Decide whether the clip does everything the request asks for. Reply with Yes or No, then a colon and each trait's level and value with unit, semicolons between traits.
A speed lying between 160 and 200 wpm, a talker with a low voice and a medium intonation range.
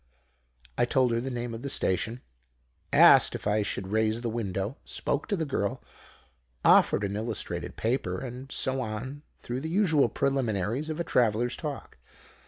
Yes: average, 165 wpm; low, 120 Hz; average, 4.0 semitones